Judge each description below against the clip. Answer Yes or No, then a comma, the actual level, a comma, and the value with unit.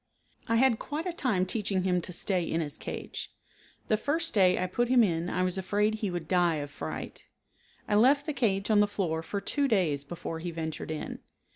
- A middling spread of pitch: Yes, average, 4.7 semitones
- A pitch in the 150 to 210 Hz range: Yes, high, 190 Hz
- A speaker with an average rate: No, fast, 215 wpm